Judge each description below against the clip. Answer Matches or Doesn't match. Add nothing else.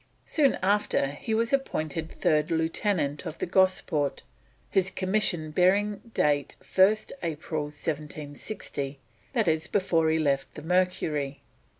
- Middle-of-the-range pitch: Matches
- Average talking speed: Doesn't match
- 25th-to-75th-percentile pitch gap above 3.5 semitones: Matches